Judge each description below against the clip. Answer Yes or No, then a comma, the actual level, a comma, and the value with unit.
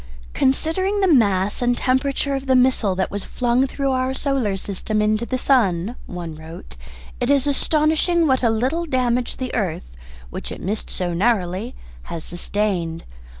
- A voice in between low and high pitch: No, high, 240 Hz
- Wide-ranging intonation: Yes, wide, 5.8 semitones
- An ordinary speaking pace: Yes, average, 160 wpm